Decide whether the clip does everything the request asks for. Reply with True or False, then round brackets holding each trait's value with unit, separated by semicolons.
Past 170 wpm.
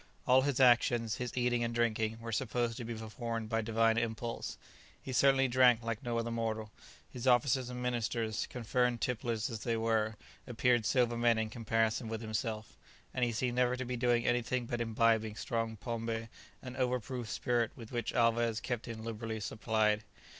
True (180 wpm)